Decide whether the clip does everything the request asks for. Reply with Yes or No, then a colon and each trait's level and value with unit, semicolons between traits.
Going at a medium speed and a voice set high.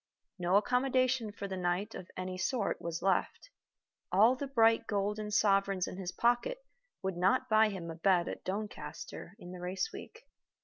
Yes: average, 170 wpm; high, 200 Hz